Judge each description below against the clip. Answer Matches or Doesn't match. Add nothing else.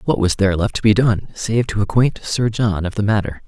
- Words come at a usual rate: Doesn't match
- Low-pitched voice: Matches